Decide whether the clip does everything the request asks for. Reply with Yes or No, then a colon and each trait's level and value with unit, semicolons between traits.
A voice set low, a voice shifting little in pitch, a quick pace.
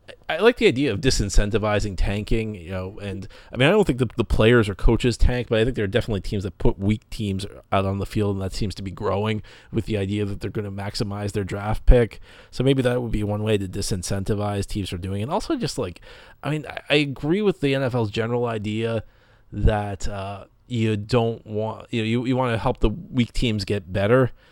No: low, 110 Hz; average, 3.0 semitones; fast, 235 wpm